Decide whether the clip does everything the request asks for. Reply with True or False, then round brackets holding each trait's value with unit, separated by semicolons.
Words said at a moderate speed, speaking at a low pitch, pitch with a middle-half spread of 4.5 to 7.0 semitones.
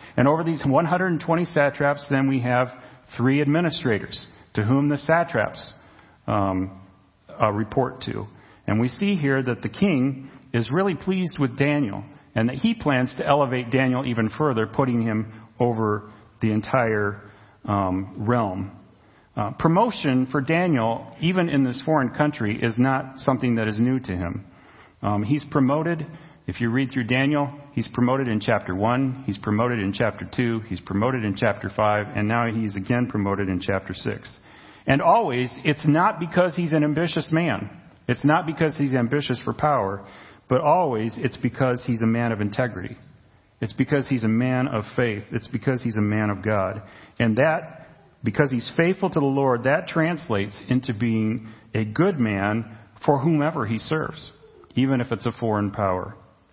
True (170 wpm; 125 Hz; 4.9 semitones)